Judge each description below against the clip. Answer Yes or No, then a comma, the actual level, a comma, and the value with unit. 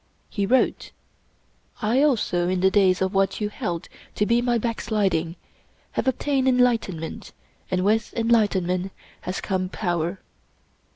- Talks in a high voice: Yes, high, 200 Hz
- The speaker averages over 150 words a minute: No, average, 140 wpm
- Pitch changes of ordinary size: Yes, average, 4.2 semitones